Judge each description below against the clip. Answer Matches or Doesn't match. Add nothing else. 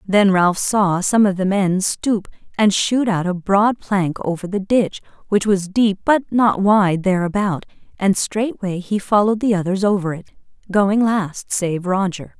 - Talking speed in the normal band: Matches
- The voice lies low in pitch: Doesn't match